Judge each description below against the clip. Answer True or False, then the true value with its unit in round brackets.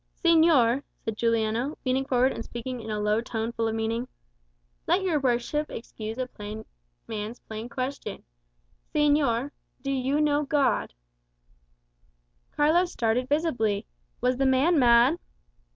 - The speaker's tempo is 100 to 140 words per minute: True (135 wpm)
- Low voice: False (250 Hz)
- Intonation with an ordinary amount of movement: True (4.3 semitones)